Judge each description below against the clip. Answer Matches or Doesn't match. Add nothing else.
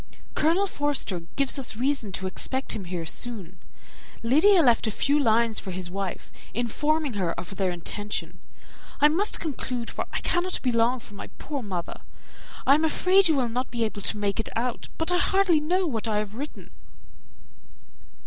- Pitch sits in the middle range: Doesn't match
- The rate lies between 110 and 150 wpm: Doesn't match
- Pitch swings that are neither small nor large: Doesn't match